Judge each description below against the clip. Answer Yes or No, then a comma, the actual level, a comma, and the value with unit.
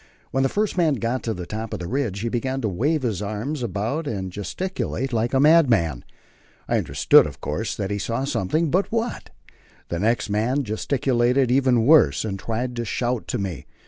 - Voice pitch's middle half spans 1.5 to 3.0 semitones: No, average, 4.7 semitones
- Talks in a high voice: No, low, 120 Hz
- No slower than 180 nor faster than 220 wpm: Yes, average, 195 wpm